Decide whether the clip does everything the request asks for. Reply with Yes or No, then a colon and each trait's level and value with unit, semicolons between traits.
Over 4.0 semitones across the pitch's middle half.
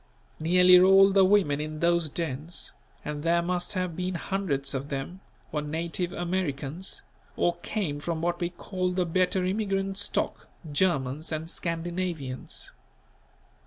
No: average, 3.1 semitones